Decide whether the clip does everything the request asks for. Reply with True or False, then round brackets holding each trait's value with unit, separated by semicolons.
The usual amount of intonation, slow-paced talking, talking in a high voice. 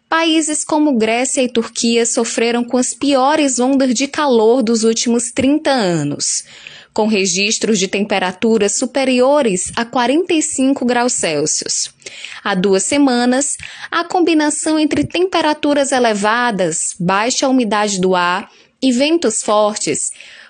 True (4.7 semitones; 115 wpm; 245 Hz)